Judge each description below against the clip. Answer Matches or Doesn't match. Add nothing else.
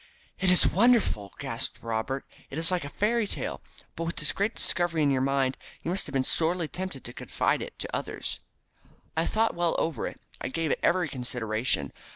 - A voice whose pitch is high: Doesn't match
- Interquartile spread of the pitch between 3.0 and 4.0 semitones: Doesn't match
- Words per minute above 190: Matches